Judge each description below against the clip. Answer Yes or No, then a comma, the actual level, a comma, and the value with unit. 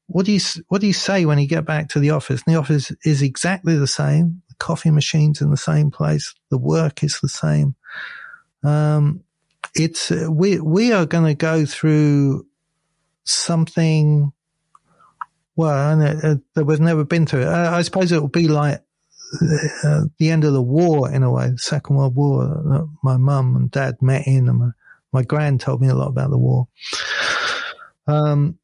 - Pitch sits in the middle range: Yes, medium, 150 Hz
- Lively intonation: No, narrow, 2.6 semitones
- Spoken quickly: No, average, 195 wpm